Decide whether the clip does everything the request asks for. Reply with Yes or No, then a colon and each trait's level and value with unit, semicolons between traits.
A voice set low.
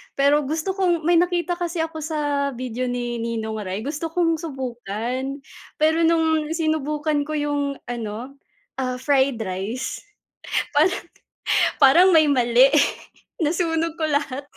No: very high, 290 Hz